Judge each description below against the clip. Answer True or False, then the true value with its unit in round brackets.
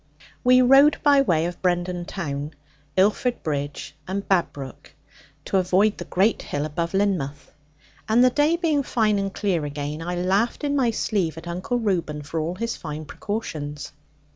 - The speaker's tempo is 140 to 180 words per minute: True (165 wpm)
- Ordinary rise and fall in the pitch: False (6.5 semitones)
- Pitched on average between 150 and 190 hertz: True (185 Hz)